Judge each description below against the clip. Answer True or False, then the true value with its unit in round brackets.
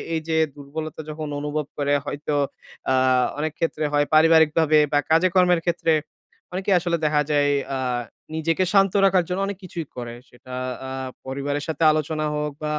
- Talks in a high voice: False (155 Hz)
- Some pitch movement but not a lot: False (2.2 semitones)